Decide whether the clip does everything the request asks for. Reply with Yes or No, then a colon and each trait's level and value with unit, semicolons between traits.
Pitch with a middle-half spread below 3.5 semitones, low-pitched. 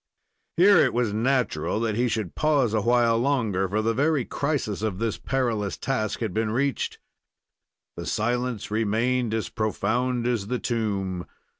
Yes: average, 2.9 semitones; low, 115 Hz